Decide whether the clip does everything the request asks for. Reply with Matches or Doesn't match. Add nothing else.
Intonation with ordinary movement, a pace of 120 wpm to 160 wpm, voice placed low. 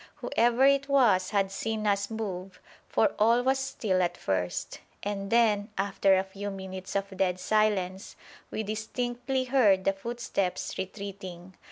Doesn't match